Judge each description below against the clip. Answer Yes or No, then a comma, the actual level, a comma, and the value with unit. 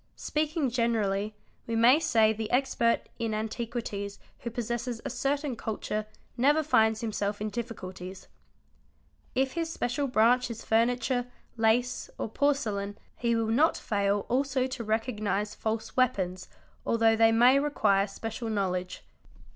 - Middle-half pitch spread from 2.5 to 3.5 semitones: Yes, average, 2.9 semitones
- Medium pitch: No, high, 230 Hz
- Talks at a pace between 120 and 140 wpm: Yes, slow, 135 wpm